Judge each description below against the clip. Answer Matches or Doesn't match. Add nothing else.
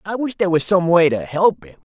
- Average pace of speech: Doesn't match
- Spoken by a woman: Doesn't match